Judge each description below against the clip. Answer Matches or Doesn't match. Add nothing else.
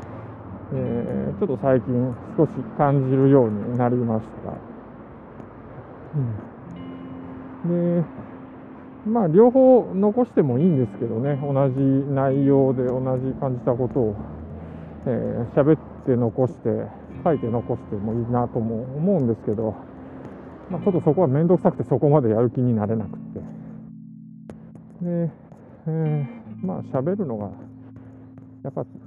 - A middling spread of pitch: Matches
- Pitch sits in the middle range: Doesn't match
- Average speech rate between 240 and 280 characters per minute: Matches